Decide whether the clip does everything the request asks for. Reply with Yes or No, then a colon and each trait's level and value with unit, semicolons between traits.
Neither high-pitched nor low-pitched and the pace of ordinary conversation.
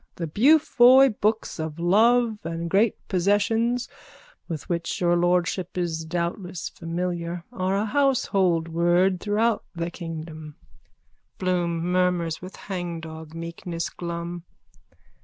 No: medium, 175 Hz; slow, 110 wpm